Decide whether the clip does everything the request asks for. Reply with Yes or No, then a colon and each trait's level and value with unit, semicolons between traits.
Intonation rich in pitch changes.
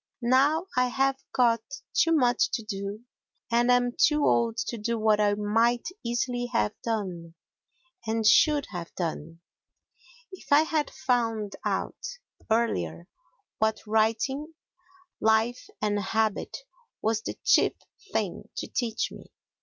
No: average, 2.9 semitones